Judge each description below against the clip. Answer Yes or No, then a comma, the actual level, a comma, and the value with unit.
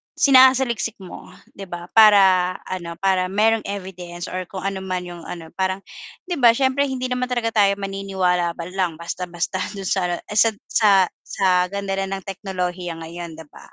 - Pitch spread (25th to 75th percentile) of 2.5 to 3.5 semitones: Yes, average, 2.9 semitones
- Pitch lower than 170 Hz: No, high, 190 Hz